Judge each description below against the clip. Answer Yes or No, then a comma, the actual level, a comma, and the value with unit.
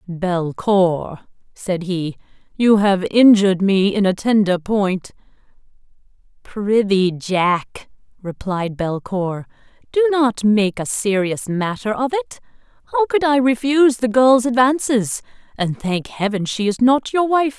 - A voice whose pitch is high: Yes, high, 215 Hz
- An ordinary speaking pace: No, slow, 130 wpm